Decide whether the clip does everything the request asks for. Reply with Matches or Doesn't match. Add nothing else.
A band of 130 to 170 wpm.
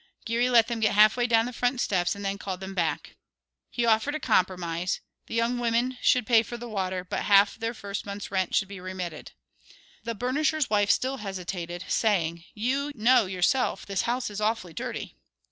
Doesn't match